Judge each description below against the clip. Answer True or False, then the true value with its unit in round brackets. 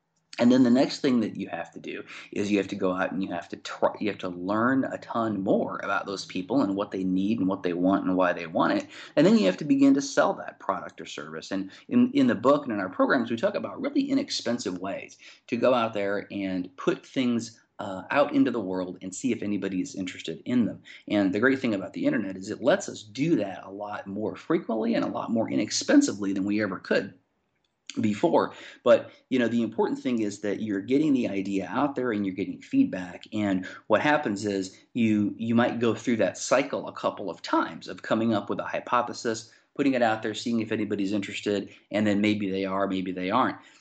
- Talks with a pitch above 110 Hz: False (105 Hz)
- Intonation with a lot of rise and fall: True (6.2 semitones)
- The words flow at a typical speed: False (235 wpm)